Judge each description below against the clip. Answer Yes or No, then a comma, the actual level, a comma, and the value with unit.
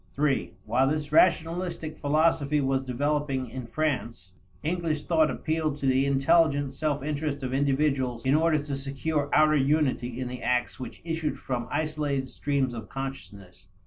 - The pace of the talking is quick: No, average, 150 wpm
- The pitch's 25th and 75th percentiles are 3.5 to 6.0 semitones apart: No, narrow, 2.6 semitones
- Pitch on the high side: No, medium, 145 Hz